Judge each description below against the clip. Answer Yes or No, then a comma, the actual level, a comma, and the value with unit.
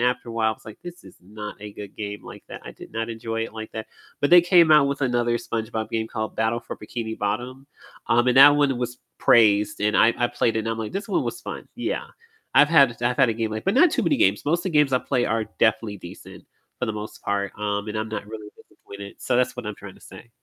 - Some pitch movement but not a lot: Yes, average, 3.0 semitones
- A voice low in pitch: Yes, low, 115 Hz